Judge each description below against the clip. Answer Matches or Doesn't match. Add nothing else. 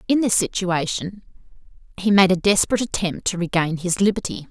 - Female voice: Matches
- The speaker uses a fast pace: Doesn't match